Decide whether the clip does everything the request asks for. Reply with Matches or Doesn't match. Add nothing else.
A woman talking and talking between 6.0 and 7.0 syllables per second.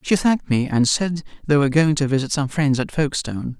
Doesn't match